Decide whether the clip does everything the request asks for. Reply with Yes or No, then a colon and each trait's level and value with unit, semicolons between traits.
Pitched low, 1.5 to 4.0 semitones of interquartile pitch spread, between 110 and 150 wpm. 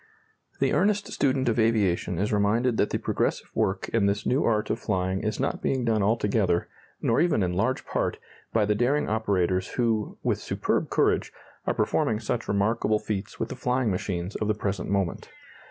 No: low, 105 Hz; average, 3.0 semitones; average, 185 wpm